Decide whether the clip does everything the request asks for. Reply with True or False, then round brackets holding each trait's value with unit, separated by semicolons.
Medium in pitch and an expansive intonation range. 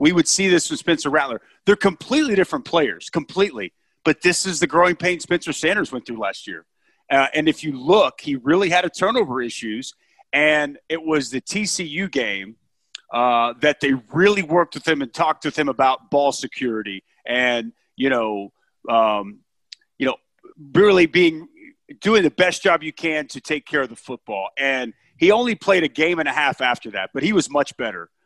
True (155 Hz; 6.0 semitones)